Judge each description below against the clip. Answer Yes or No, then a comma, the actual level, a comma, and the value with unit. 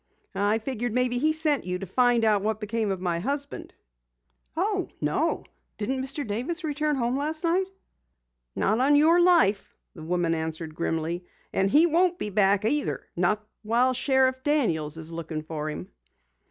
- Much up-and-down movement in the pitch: Yes, wide, 8.0 semitones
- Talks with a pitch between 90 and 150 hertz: No, high, 225 Hz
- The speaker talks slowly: No, average, 165 wpm